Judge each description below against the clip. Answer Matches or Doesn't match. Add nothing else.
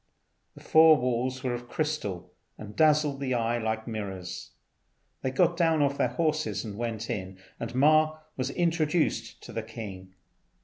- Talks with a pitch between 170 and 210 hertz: Doesn't match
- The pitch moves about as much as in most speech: Doesn't match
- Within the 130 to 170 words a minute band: Matches